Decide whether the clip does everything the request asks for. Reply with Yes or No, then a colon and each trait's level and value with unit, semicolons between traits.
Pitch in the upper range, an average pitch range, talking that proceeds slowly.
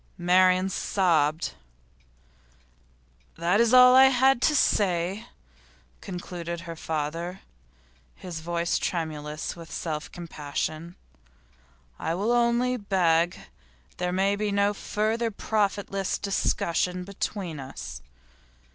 No: medium, 180 Hz; average, 3.6 semitones; slow, 100 wpm